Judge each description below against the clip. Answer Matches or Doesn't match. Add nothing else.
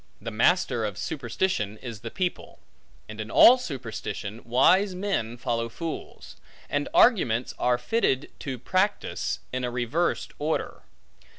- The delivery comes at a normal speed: Doesn't match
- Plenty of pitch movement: Matches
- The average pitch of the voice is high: Doesn't match